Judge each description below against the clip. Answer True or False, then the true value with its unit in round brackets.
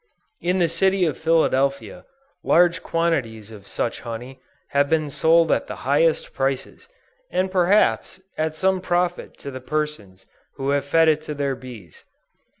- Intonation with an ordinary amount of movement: True (4.2 semitones)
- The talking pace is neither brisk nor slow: True (150 wpm)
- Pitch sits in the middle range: True (150 Hz)